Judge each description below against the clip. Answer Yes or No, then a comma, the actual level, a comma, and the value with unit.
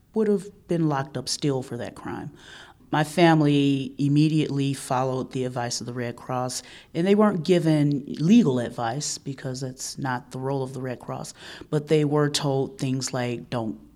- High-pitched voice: No, low, 135 Hz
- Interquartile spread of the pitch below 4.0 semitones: Yes, average, 3.1 semitones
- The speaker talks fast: No, average, 175 wpm